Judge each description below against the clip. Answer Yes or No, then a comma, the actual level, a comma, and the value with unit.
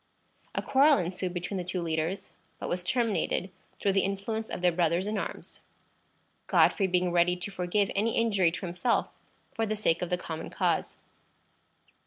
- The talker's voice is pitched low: No, medium, 185 Hz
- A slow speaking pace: No, average, 170 wpm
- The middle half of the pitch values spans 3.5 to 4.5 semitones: No, average, 2.9 semitones